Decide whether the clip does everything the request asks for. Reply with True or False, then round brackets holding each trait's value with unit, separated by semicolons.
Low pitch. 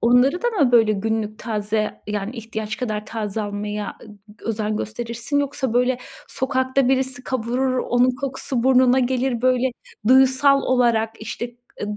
False (245 Hz)